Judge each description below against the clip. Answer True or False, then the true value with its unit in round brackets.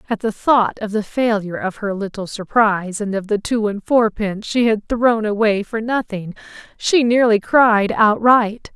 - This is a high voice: True (215 Hz)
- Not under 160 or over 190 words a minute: True (180 wpm)